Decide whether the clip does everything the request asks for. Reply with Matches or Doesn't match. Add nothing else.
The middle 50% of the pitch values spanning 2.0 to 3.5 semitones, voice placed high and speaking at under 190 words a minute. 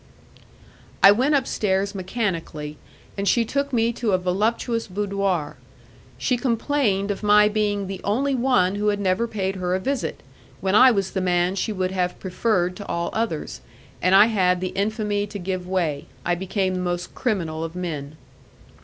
Matches